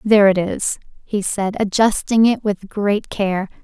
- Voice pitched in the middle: No, high, 205 Hz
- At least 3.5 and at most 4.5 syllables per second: Yes, 4.1 syllables/s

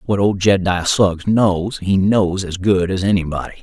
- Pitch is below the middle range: Yes, very low, 95 Hz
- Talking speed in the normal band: Yes, average, 180 wpm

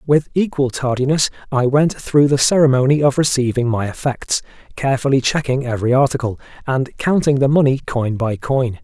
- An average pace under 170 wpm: Yes, average, 155 wpm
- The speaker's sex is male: Yes, male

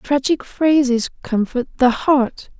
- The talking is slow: Yes, slow, 115 wpm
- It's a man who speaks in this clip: No, female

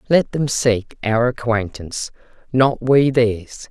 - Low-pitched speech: Yes, low, 120 Hz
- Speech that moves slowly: Yes, slow, 130 wpm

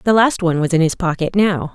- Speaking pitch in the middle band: Yes, medium, 180 Hz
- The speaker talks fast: Yes, fast, 275 wpm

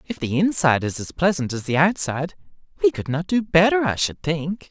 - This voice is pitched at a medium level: Yes, medium, 165 Hz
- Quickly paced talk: Yes, fast, 215 wpm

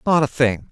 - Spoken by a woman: No, male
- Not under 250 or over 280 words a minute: Yes, fast, 255 wpm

